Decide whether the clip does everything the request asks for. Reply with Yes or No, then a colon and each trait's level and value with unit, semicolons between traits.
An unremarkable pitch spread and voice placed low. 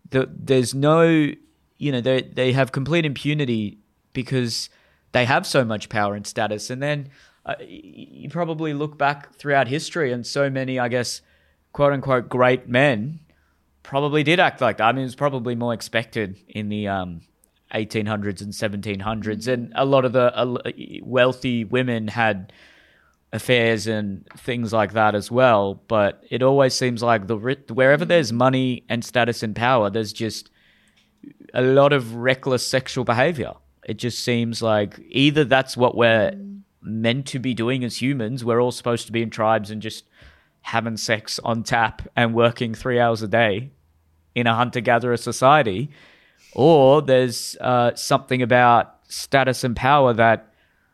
Yes: average, 3.1 semitones; low, 120 Hz